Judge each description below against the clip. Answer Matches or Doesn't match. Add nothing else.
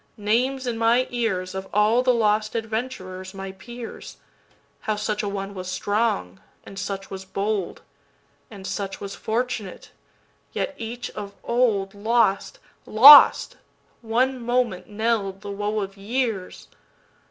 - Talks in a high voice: Matches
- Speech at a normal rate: Doesn't match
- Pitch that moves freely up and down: Doesn't match